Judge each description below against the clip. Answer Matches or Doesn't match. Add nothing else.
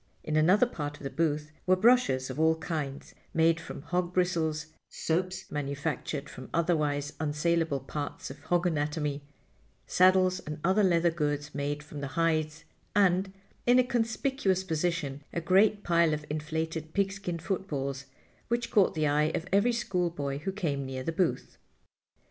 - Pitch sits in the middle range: Matches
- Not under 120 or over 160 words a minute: Matches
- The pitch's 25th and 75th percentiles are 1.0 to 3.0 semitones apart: Doesn't match